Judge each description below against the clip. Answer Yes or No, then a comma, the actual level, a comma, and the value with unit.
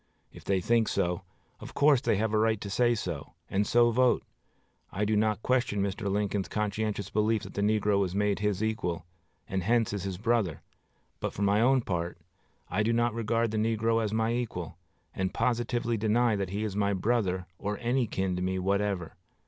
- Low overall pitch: Yes, low, 105 Hz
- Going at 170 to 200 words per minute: Yes, average, 195 wpm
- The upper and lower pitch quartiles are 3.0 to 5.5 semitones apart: No, narrow, 2.6 semitones